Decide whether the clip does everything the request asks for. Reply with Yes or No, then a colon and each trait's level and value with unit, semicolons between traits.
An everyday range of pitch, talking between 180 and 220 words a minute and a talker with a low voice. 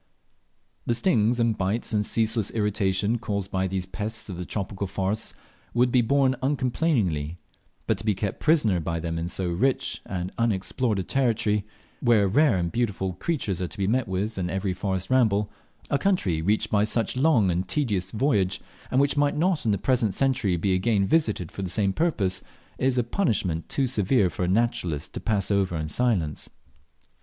Yes: average, 4.5 semitones; average, 185 wpm; low, 105 Hz